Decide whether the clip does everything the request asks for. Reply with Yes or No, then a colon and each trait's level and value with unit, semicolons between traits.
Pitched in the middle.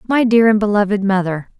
No: high, 205 Hz